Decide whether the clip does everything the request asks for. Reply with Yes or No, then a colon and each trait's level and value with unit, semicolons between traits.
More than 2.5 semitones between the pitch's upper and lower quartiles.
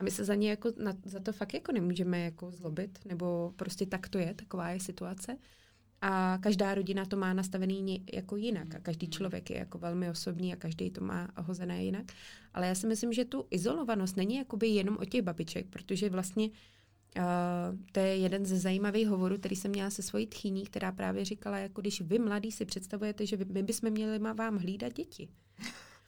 Yes: average, 2.9 semitones